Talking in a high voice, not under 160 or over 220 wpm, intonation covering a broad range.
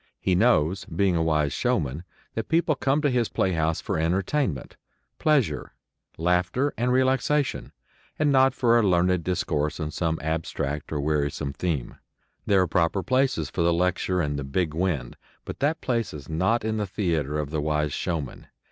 No: very low, 90 Hz; average, 170 wpm; wide, 7.2 semitones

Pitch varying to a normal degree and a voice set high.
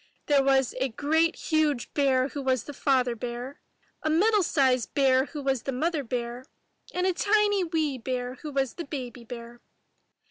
Yes: average, 3.7 semitones; very high, 270 Hz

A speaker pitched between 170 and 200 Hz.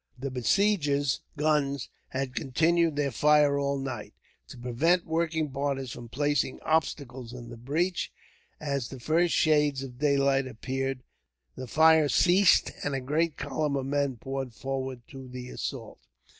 No: medium, 140 Hz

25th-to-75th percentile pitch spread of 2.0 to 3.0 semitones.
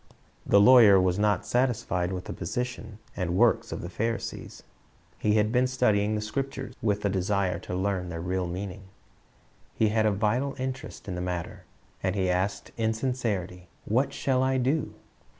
No: average, 4.9 semitones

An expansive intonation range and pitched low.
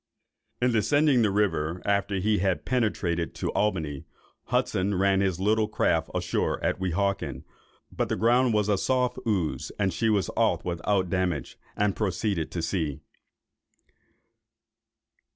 No: average, 3.3 semitones; low, 100 Hz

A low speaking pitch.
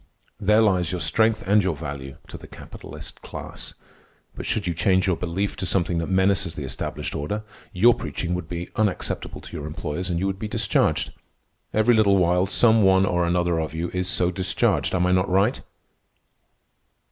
Yes: very low, 90 Hz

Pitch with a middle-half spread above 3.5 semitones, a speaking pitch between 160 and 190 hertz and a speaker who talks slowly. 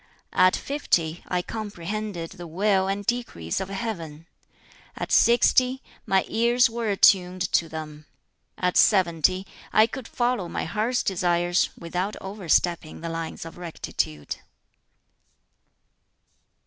Yes: average, 4.3 semitones; medium, 185 Hz; slow, 115 wpm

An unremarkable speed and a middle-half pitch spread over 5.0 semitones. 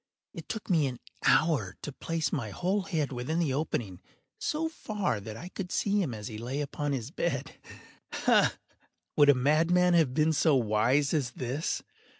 Yes: average, 170 wpm; wide, 5.5 semitones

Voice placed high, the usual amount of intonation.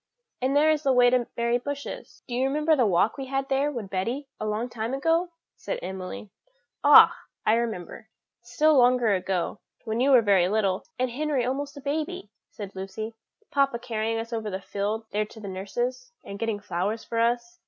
Yes: high, 235 Hz; average, 4.3 semitones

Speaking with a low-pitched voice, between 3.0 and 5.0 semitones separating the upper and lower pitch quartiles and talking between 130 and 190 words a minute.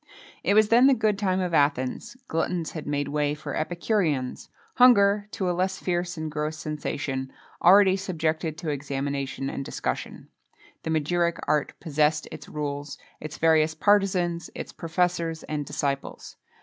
No: medium, 160 Hz; average, 3.9 semitones; average, 150 wpm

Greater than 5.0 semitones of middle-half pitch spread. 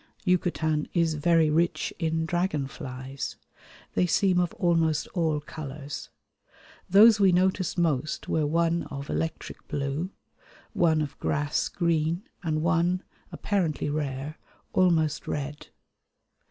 No: average, 2.7 semitones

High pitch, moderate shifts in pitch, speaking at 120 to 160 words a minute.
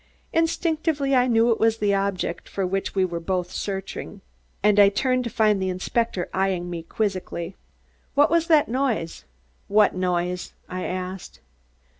Yes: high, 200 Hz; average, 4.5 semitones; average, 155 wpm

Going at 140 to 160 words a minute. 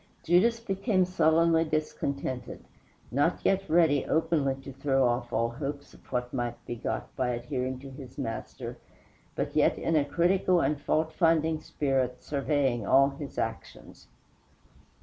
Yes: average, 145 wpm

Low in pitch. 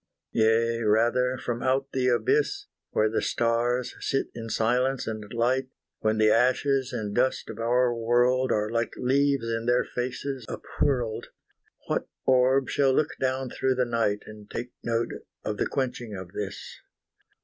Yes: low, 120 Hz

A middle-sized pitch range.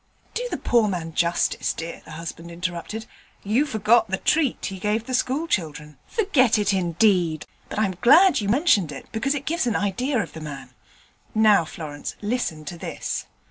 No: wide, 6.6 semitones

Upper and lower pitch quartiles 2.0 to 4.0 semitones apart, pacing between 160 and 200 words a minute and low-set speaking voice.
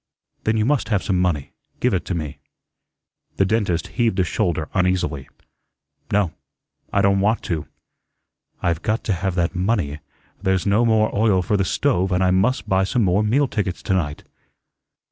Yes: average, 3.2 semitones; average, 175 wpm; very low, 95 Hz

